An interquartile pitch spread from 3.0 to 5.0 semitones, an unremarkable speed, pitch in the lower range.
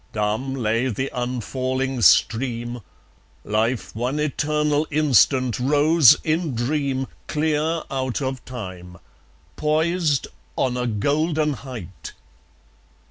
No: average, 3.9 semitones; slow, 95 wpm; low, 130 Hz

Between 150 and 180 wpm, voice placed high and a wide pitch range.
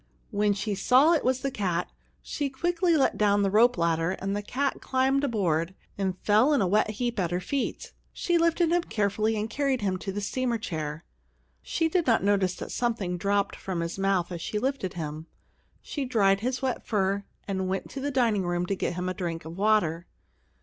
No: fast, 205 wpm; high, 205 Hz; wide, 5.8 semitones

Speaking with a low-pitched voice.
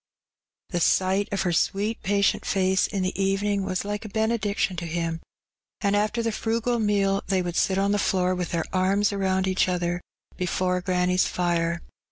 No: high, 190 Hz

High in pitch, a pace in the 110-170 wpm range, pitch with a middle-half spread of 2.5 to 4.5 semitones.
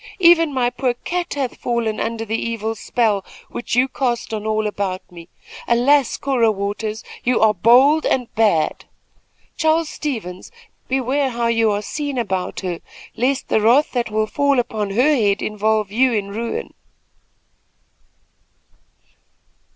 Yes: high, 230 Hz; average, 145 wpm; average, 3.8 semitones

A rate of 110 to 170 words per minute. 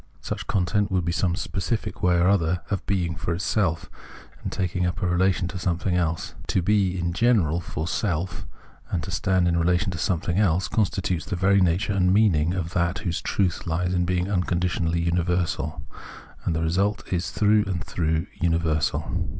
No: average, 190 wpm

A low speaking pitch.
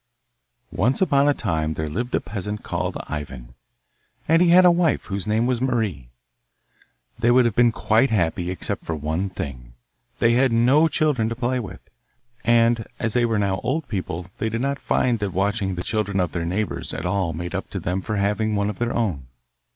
Yes: low, 110 Hz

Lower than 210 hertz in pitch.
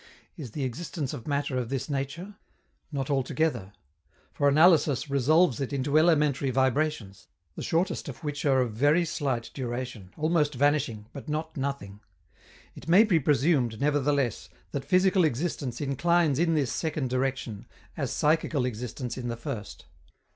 Yes: medium, 140 Hz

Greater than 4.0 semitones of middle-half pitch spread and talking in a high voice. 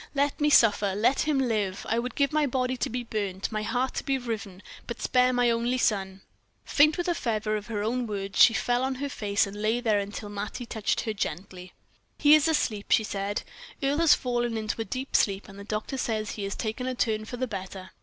No: average, 3.7 semitones; high, 225 Hz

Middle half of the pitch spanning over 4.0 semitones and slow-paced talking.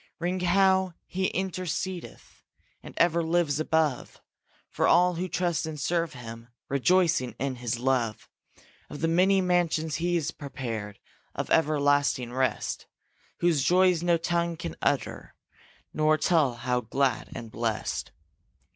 Yes: average, 5.2 semitones; slow, 130 wpm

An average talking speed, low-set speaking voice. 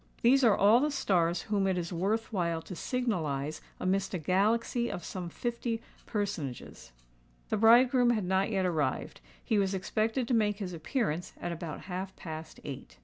No: average, 170 wpm; high, 195 Hz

